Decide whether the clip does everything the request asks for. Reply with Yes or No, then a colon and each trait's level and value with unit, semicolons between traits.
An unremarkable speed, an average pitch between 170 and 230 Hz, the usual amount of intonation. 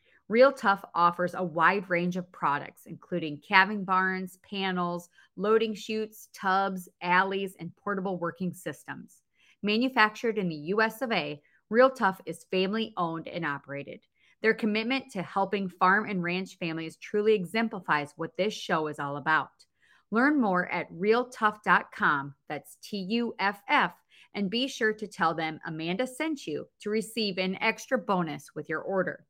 Yes: average, 150 wpm; high, 190 Hz; average, 3.9 semitones